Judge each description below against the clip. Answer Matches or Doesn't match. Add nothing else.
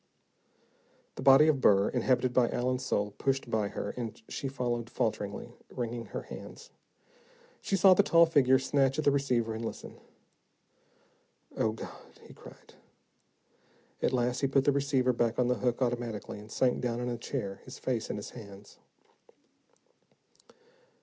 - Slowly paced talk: Doesn't match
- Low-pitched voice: Matches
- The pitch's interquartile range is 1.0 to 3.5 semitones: Matches